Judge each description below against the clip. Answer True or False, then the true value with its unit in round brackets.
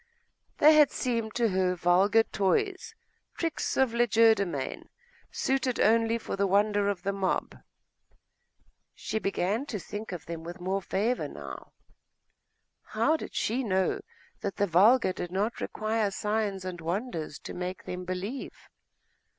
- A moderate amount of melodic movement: True (3.8 semitones)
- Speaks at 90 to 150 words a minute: True (140 wpm)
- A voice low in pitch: False (205 Hz)